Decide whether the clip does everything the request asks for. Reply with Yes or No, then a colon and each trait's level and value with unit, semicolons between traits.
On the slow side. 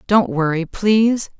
Yes: slow, 130 wpm